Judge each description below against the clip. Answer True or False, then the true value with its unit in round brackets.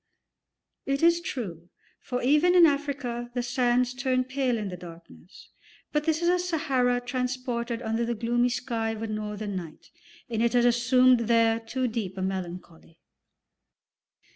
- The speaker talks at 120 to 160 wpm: True (155 wpm)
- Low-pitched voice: False (240 Hz)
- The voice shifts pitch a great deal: False (2.7 semitones)